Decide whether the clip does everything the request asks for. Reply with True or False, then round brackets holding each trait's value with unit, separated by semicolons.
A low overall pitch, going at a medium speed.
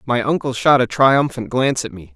False (125 Hz; 220 wpm)